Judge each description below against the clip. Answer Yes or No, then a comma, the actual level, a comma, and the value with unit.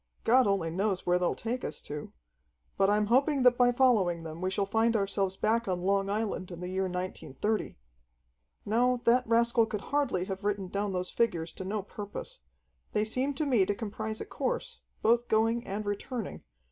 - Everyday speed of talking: Yes, average, 185 wpm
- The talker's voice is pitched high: Yes, high, 210 Hz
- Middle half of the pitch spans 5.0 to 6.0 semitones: No, average, 3.7 semitones